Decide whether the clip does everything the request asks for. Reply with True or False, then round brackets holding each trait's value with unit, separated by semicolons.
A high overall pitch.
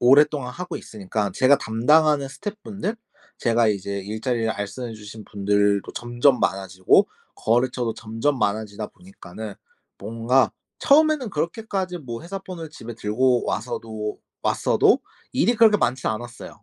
False (120 Hz)